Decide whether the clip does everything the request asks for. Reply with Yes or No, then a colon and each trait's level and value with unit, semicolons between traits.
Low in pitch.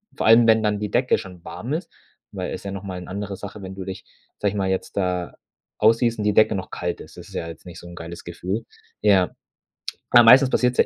Yes: low, 100 Hz